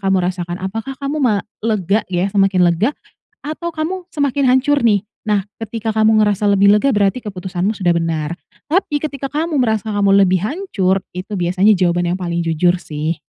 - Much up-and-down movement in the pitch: Yes, wide, 5.8 semitones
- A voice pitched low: No, high, 200 Hz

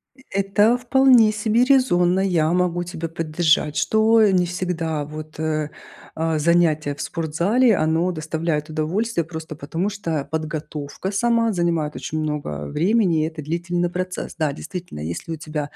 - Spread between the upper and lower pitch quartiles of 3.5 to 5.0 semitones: Yes, average, 3.8 semitones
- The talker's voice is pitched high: No, medium, 170 Hz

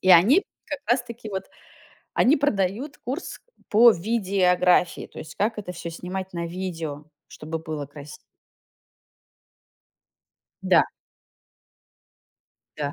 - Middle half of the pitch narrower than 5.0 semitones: No, wide, 5.4 semitones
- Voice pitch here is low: No, medium, 185 Hz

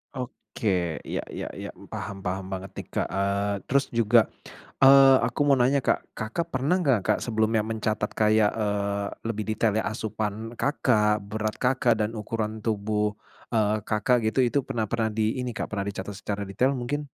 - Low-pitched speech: Yes, low, 110 Hz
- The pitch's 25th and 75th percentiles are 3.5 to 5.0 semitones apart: No, average, 3.1 semitones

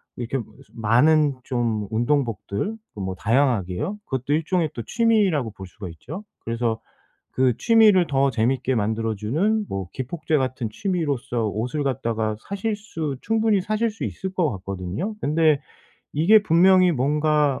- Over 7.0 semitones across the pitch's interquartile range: Yes, wide, 8.0 semitones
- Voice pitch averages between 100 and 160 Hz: Yes, medium, 140 Hz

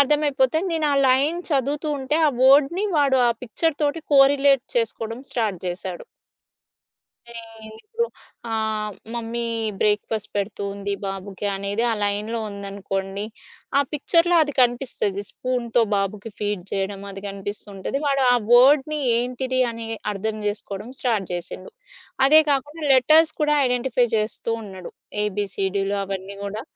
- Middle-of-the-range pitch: No, high, 230 Hz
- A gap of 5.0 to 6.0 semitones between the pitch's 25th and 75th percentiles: Yes, wide, 5.5 semitones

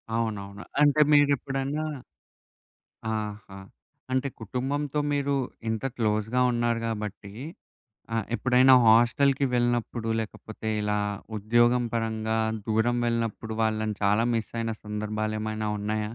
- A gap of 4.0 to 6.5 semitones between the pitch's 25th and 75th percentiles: No, narrow, 2.6 semitones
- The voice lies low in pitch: Yes, low, 115 Hz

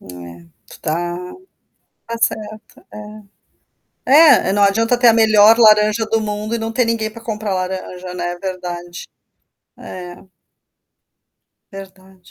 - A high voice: Yes, high, 205 Hz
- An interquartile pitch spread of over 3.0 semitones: Yes, average, 3.6 semitones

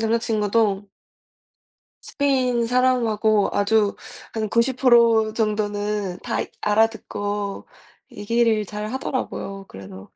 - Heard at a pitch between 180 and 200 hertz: No, high, 215 Hz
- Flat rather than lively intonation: Yes, narrow, 2.2 semitones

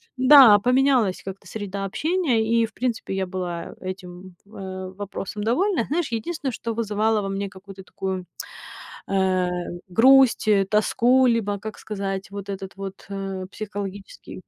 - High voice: Yes, high, 205 Hz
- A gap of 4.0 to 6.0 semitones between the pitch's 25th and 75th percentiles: No, average, 3.3 semitones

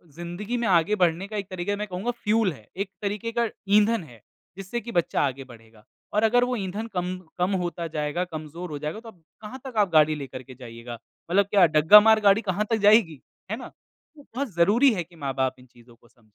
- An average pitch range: No, wide, 5.9 semitones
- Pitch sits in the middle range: Yes, medium, 180 Hz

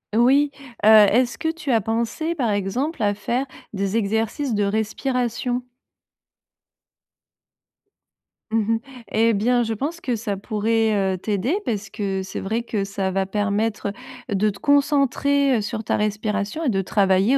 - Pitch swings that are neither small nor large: Yes, average, 3.6 semitones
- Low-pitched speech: No, high, 220 Hz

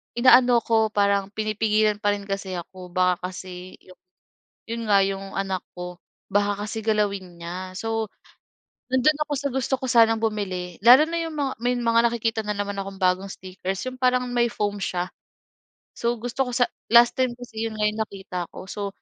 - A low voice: No, high, 210 Hz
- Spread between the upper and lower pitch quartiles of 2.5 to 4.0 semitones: Yes, average, 3.6 semitones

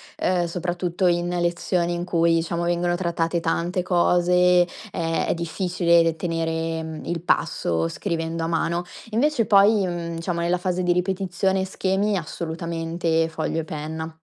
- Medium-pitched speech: Yes, medium, 170 Hz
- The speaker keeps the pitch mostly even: Yes, narrow, 1.5 semitones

